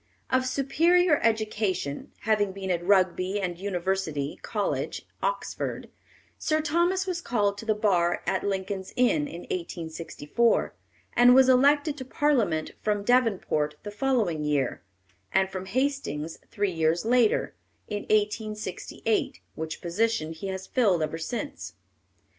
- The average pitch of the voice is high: Yes, high, 205 Hz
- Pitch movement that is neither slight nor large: No, wide, 6.2 semitones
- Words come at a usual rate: No, slow, 130 wpm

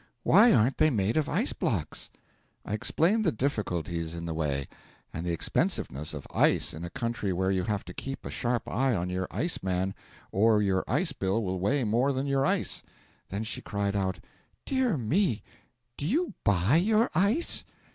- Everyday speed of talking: Yes, average, 185 wpm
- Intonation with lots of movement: Yes, wide, 7.2 semitones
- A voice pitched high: No, low, 110 Hz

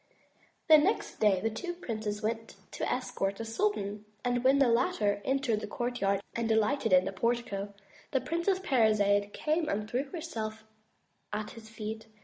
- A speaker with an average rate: Yes, average, 155 wpm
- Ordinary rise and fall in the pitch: Yes, average, 4.2 semitones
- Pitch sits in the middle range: No, high, 225 Hz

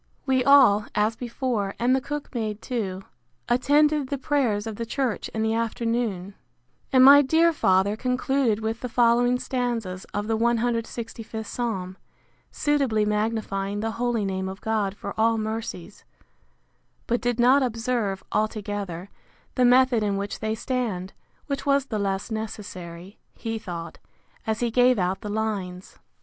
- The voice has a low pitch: No, high, 225 Hz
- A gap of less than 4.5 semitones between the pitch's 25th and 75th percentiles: Yes, average, 3.4 semitones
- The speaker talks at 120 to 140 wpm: No, average, 150 wpm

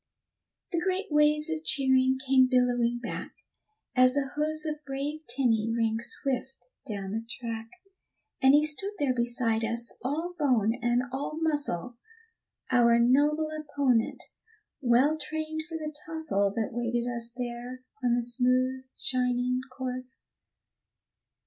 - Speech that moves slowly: Yes, slow, 130 wpm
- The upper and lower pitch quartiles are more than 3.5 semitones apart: Yes, average, 3.9 semitones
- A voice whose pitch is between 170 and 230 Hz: No, very high, 255 Hz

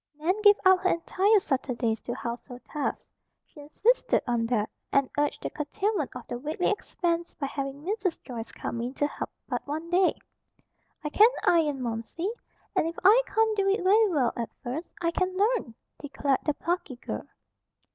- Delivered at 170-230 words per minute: Yes, average, 175 wpm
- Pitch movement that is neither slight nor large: No, wide, 6.4 semitones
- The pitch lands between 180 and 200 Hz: No, very high, 310 Hz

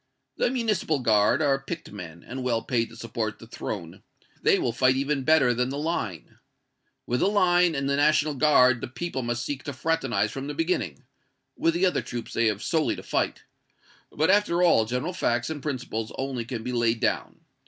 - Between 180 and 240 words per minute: Yes, average, 195 wpm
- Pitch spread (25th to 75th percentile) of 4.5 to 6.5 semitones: Yes, average, 5.1 semitones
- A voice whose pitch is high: No, low, 130 Hz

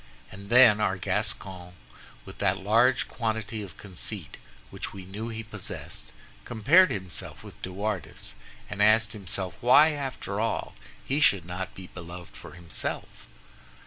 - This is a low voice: Yes, low, 105 Hz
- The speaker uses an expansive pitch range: No, average, 3.2 semitones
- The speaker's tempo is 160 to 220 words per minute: No, average, 145 wpm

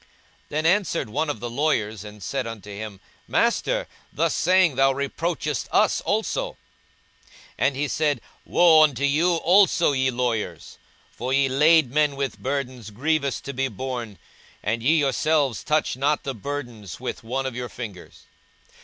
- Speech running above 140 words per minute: Yes, average, 160 wpm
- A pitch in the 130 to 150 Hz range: Yes, low, 135 Hz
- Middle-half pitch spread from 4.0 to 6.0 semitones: Yes, average, 4.5 semitones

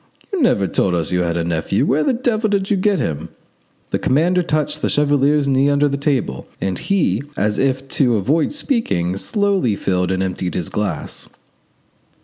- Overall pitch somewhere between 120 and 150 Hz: Yes, low, 135 Hz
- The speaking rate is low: No, average, 180 wpm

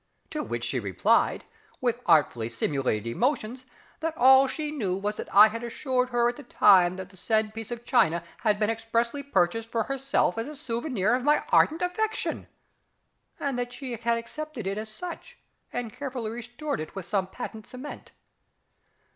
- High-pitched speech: Yes, high, 230 Hz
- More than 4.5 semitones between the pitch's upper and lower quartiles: Yes, average, 4.9 semitones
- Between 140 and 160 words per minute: No, average, 170 wpm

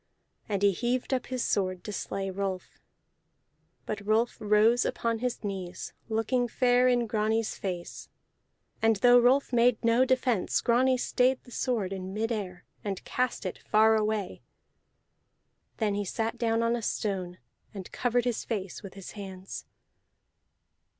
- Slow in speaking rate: No, average, 145 wpm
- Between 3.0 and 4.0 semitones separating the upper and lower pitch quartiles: Yes, average, 3.6 semitones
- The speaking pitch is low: No, high, 220 Hz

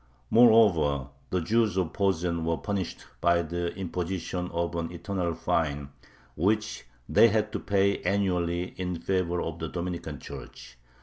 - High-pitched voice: No, very low, 90 Hz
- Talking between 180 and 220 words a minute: No, average, 140 wpm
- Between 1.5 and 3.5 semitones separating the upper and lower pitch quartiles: Yes, average, 2.7 semitones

